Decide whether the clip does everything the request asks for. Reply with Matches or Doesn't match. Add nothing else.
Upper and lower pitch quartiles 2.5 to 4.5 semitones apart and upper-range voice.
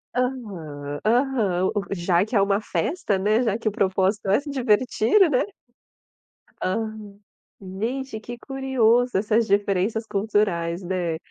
Matches